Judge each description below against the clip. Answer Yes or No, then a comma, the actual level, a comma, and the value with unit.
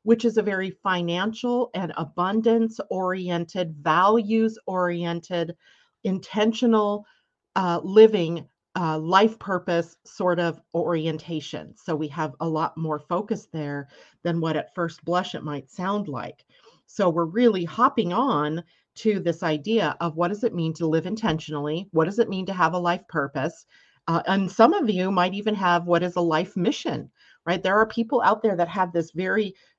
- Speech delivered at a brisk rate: No, average, 170 wpm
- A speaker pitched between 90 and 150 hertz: No, medium, 180 Hz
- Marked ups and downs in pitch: No, average, 4.5 semitones